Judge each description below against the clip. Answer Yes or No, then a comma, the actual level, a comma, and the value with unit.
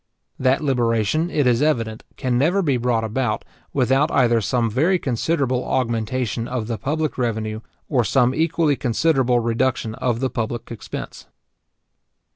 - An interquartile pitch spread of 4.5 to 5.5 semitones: No, average, 3.3 semitones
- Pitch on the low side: Yes, low, 125 Hz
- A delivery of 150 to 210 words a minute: No, average, 140 wpm